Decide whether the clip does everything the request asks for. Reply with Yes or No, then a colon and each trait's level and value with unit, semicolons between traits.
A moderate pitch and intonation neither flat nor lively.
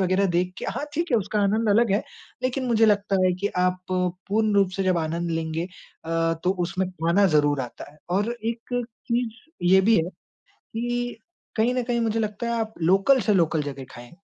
No: high, 200 Hz; average, 4.9 semitones